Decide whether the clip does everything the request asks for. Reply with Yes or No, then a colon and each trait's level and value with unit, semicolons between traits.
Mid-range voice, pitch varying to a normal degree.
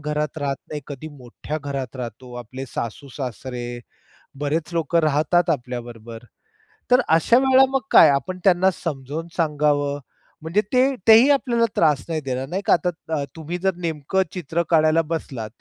Yes: medium, 150 Hz; average, 4.3 semitones